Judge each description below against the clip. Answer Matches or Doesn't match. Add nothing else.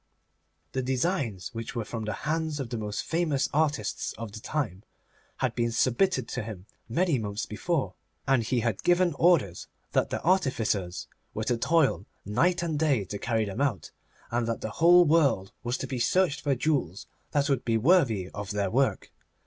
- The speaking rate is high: Doesn't match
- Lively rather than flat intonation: Matches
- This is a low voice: Matches